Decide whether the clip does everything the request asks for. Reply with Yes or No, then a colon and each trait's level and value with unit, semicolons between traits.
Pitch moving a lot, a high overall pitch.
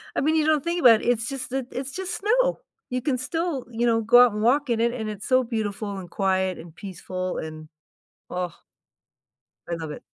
Yes: wide, 6.0 semitones; high, 235 Hz